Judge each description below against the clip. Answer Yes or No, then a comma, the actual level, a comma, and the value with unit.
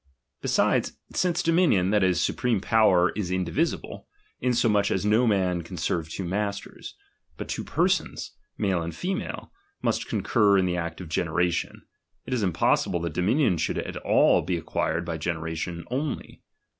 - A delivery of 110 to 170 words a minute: Yes, average, 155 wpm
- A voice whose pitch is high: No, very low, 95 Hz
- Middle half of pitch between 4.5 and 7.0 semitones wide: No, average, 4.1 semitones